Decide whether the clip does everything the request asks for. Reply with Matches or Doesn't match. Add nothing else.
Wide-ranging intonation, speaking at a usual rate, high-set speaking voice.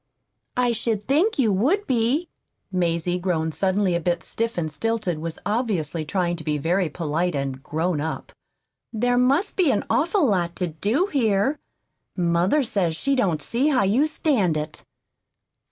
Matches